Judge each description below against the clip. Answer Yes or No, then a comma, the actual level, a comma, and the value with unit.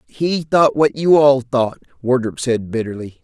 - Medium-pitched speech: No, low, 130 Hz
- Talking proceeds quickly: No, average, 165 wpm